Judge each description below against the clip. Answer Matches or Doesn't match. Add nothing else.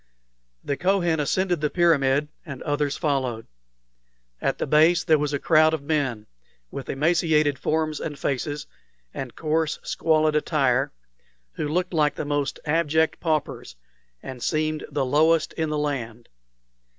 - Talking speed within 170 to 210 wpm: Doesn't match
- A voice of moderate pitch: Matches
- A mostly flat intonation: Matches